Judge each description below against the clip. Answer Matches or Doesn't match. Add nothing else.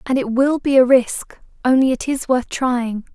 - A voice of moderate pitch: Doesn't match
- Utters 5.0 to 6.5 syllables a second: Doesn't match